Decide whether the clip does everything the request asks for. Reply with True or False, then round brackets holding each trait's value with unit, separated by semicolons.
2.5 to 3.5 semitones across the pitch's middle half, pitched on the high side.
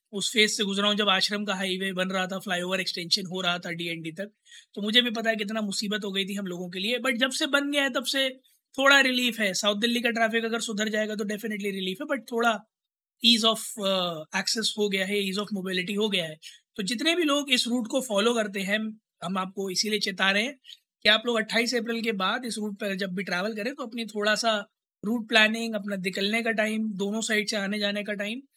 True (3.0 semitones; 215 Hz)